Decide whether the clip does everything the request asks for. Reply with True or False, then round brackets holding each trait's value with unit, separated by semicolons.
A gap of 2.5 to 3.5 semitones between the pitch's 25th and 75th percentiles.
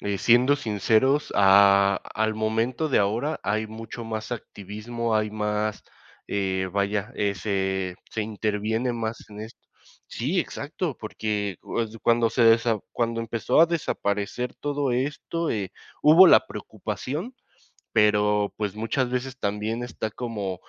True (2.9 semitones)